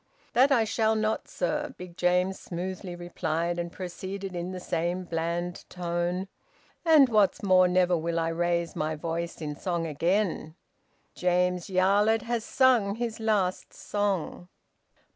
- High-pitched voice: No, medium, 180 Hz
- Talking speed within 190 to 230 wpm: No, average, 140 wpm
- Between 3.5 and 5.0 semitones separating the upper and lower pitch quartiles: No, average, 2.8 semitones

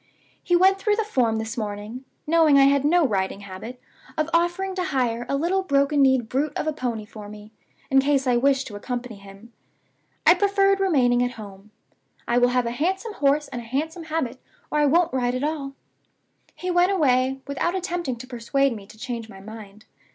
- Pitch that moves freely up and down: Yes, wide, 5.8 semitones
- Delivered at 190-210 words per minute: Yes, average, 200 wpm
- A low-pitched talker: No, very high, 270 Hz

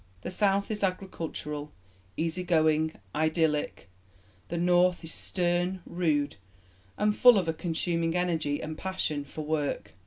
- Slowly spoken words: Yes, slow, 130 wpm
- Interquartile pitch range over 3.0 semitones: No, average, 2.7 semitones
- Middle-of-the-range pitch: Yes, medium, 165 Hz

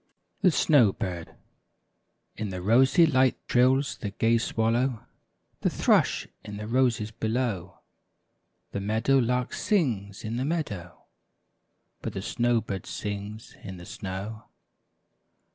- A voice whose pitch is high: No, low, 110 Hz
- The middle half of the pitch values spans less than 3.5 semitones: No, average, 4.0 semitones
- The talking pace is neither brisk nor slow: No, slow, 125 wpm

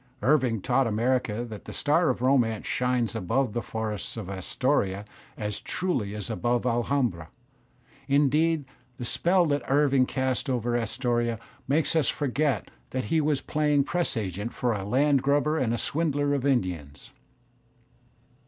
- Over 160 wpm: No, average, 145 wpm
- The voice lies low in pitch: Yes, low, 125 Hz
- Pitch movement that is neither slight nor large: Yes, average, 4.3 semitones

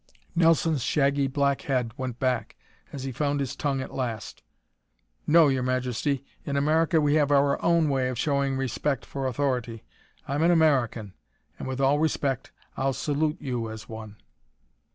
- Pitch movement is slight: Yes, narrow, 2.3 semitones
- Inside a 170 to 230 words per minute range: No, average, 160 wpm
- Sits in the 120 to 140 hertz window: Yes, low, 135 Hz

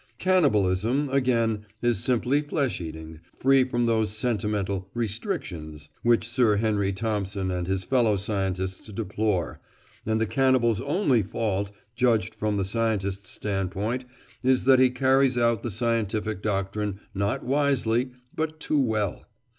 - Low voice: Yes, low, 110 Hz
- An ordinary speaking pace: No, slow, 130 wpm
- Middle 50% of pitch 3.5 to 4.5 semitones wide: Yes, average, 4.2 semitones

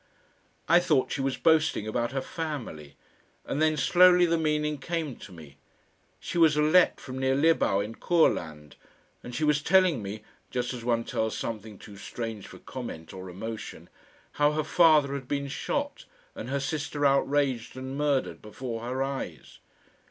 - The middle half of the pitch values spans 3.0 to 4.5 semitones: No, average, 5.3 semitones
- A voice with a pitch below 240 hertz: Yes, low, 135 Hz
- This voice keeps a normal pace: Yes, average, 165 wpm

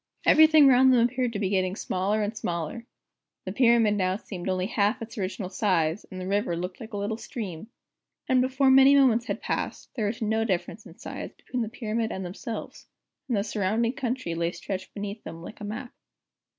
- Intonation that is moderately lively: Yes, average, 4.1 semitones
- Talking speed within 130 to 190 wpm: No, average, 200 wpm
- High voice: Yes, high, 215 Hz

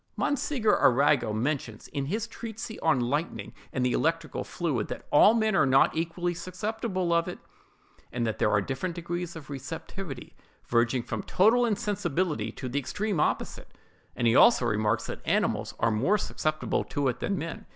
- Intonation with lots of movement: Yes, wide, 7.1 semitones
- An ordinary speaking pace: Yes, average, 170 wpm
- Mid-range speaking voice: Yes, medium, 160 Hz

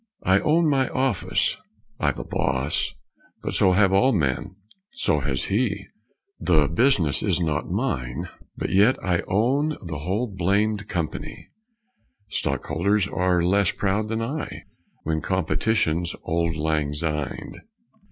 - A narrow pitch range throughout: No, average, 5.3 semitones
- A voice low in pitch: Yes, very low, 95 Hz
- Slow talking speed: Yes, slow, 130 wpm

